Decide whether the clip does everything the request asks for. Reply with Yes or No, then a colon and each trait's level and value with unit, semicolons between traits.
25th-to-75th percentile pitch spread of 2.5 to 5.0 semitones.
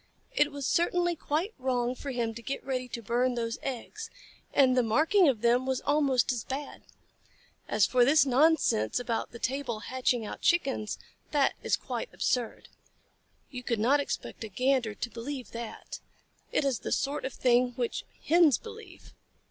Yes: average, 3.3 semitones